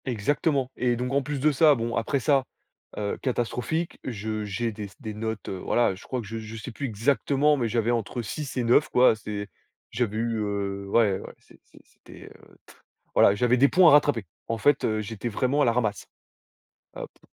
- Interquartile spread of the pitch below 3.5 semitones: No, average, 3.9 semitones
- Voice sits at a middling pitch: No, low, 115 Hz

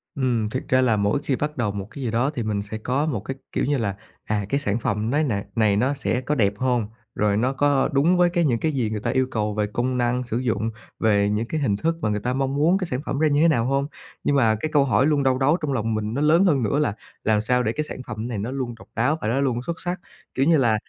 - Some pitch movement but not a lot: Yes, average, 4.6 semitones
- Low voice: Yes, low, 125 Hz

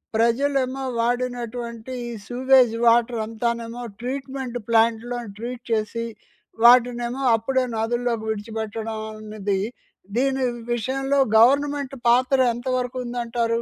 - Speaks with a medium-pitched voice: No, high, 240 Hz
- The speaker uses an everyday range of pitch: No, narrow, 2.0 semitones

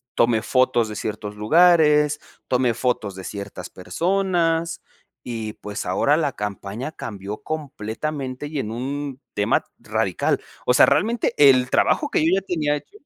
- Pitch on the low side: Yes, low, 130 Hz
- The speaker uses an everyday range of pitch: No, wide, 6.4 semitones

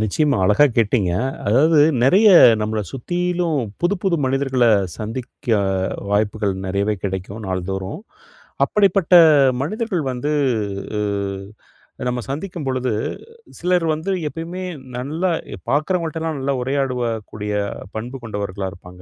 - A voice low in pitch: Yes, low, 130 Hz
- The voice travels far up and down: Yes, wide, 7.5 semitones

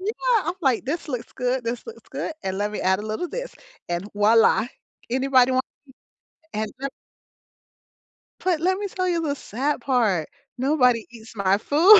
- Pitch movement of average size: No, wide, 7.4 semitones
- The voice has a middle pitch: No, very high, 255 Hz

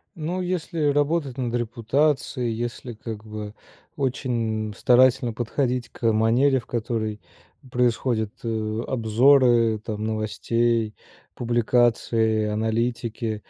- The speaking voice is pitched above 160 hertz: No, low, 115 Hz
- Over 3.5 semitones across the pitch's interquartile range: No, narrow, 2.6 semitones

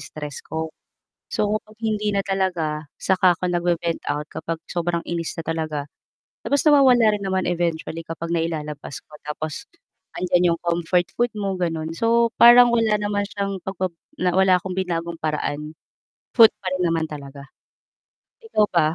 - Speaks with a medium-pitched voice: Yes, medium, 175 Hz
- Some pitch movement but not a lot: Yes, average, 3.9 semitones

